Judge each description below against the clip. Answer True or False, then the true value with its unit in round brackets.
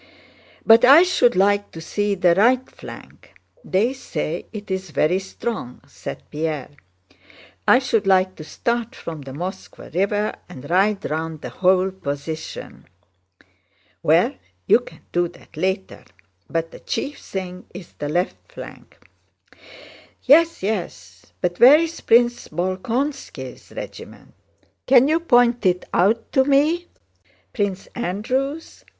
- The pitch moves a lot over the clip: True (5.7 semitones)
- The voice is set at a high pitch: True (195 Hz)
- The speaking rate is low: True (130 wpm)